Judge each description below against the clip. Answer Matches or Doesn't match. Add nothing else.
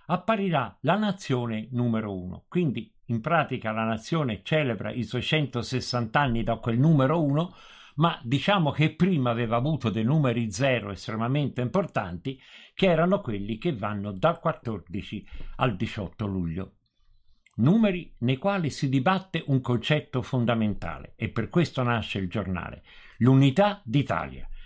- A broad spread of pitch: Matches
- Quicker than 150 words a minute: Doesn't match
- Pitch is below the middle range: Matches